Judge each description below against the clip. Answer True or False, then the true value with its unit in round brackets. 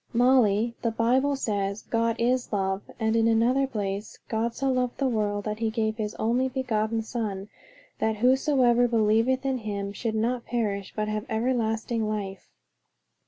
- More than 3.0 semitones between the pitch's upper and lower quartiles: False (2.5 semitones)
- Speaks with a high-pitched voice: True (225 Hz)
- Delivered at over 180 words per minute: False (160 wpm)